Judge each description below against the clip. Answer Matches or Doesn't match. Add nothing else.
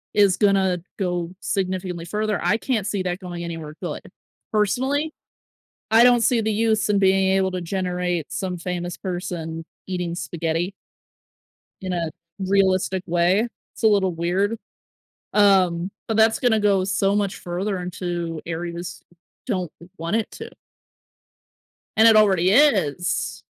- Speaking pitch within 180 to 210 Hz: Matches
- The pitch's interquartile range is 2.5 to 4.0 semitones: Matches